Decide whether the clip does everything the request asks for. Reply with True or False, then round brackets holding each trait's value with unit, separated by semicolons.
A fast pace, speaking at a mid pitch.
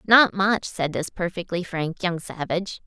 False (165 wpm; 180 Hz)